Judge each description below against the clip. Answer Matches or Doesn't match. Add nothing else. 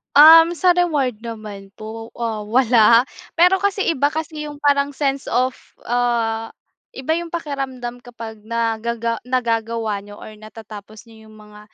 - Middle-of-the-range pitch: Doesn't match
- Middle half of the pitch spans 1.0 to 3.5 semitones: Doesn't match